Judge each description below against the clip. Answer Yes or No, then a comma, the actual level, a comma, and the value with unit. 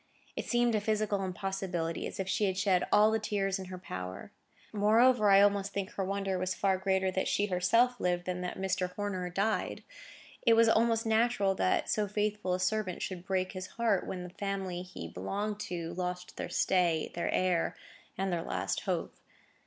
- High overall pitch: Yes, high, 195 Hz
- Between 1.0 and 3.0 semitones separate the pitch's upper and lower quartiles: Yes, narrow, 2.4 semitones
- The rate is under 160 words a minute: No, average, 190 wpm